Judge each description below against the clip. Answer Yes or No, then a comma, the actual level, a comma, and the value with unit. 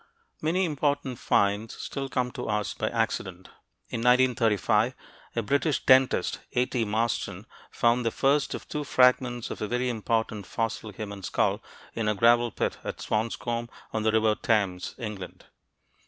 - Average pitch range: Yes, average, 3.0 semitones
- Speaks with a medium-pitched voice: No, low, 115 Hz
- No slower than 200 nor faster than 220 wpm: No, average, 155 wpm